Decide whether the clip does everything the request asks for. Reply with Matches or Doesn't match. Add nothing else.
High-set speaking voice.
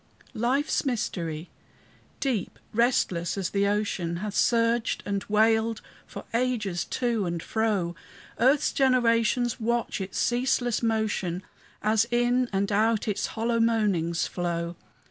Matches